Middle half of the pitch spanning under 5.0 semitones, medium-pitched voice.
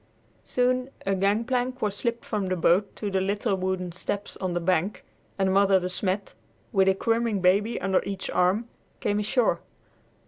No: average, 2.8 semitones; high, 195 Hz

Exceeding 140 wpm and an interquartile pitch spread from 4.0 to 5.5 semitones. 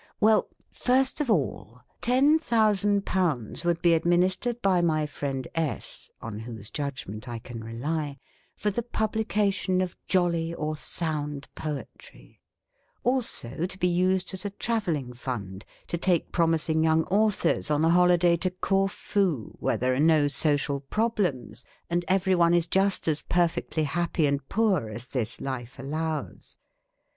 Yes: average, 150 wpm; average, 5.2 semitones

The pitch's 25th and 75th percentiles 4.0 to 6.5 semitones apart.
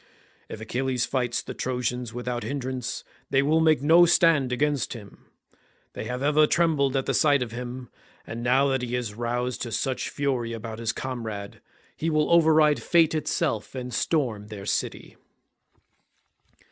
No: average, 3.6 semitones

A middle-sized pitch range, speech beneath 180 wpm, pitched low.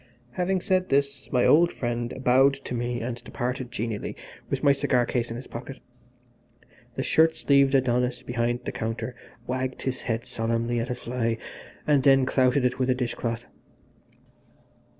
No: narrow, 2.2 semitones; average, 165 wpm; low, 125 Hz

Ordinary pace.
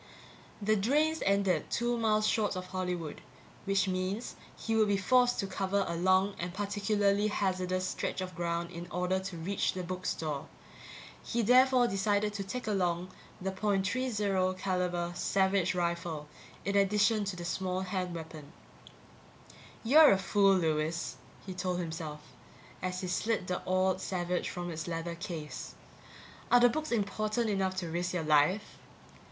Yes: average, 155 wpm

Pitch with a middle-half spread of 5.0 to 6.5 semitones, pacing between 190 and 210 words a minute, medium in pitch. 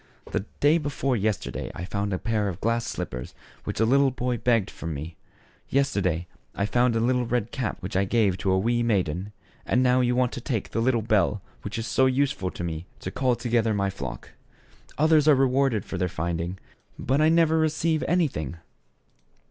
No: wide, 5.4 semitones; average, 195 wpm; low, 115 Hz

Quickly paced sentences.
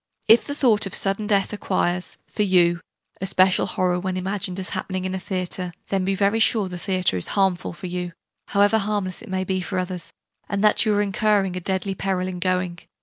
Yes: fast, 210 wpm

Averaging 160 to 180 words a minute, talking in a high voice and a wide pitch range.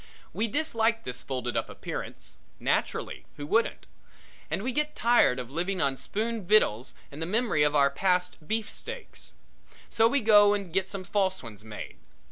Yes: average, 165 wpm; high, 195 Hz; wide, 7.6 semitones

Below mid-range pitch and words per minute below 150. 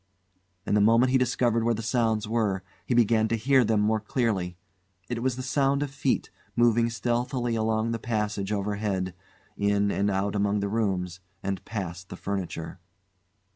No: low, 110 Hz; average, 170 wpm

